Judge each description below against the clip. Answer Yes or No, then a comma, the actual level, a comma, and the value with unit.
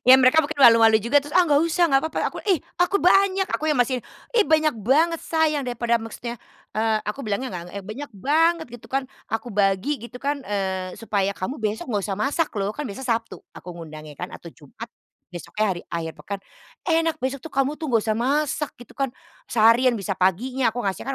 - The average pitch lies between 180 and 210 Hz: No, high, 245 Hz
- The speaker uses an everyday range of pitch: No, wide, 6.1 semitones